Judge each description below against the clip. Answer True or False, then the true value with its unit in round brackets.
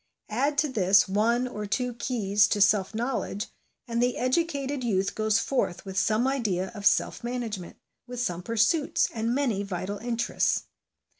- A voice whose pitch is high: True (230 Hz)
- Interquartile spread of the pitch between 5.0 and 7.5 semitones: False (3.6 semitones)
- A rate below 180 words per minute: True (155 wpm)